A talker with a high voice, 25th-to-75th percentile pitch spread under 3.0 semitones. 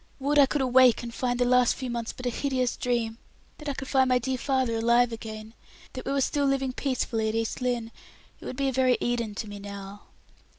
Yes: high, 245 Hz; narrow, 2.5 semitones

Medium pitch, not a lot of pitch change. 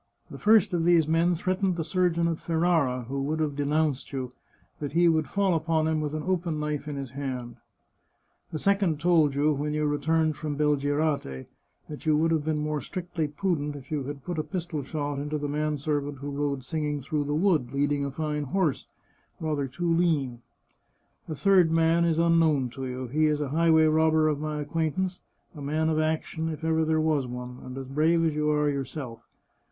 Yes: medium, 155 Hz; narrow, 2.3 semitones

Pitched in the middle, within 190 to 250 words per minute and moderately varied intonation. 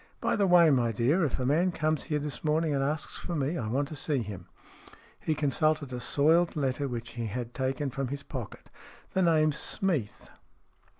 Yes: medium, 145 Hz; average, 200 wpm; average, 3.7 semitones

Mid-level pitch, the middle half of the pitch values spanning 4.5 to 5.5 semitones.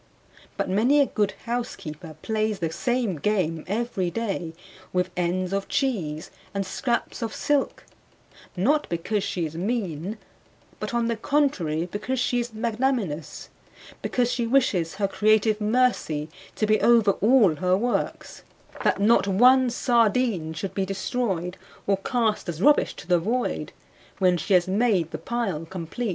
No: high, 210 Hz; average, 5.0 semitones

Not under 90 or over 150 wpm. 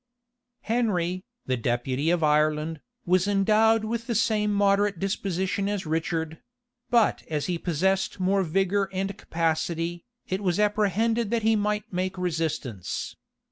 Yes: slow, 135 wpm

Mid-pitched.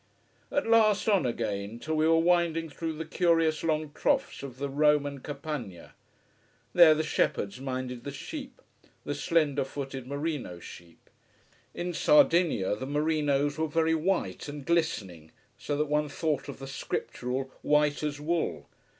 Yes: medium, 150 Hz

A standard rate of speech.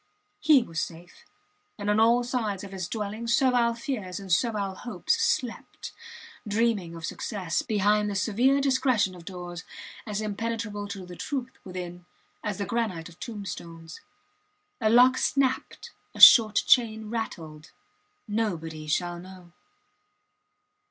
No: slow, 130 wpm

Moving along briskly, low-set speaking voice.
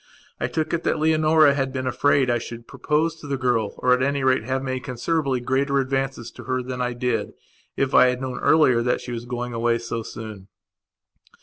Yes: fast, 210 wpm; low, 130 Hz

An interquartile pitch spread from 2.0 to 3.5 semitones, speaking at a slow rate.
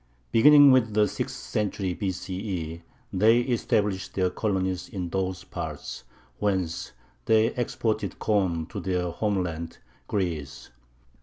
Yes: average, 3.2 semitones; slow, 110 wpm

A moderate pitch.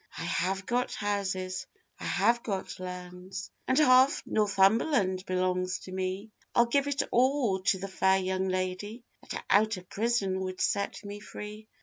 No: high, 195 Hz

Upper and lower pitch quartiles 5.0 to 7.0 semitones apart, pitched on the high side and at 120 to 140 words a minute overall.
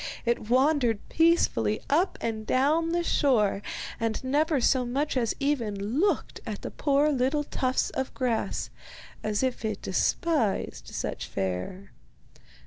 Yes: average, 5.3 semitones; very high, 255 Hz; slow, 135 wpm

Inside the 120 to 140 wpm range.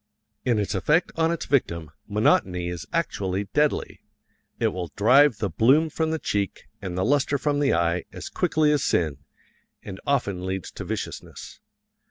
No: average, 165 wpm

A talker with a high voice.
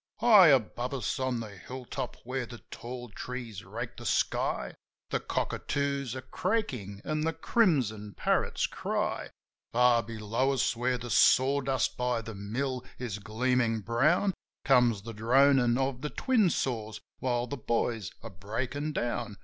No: low, 125 Hz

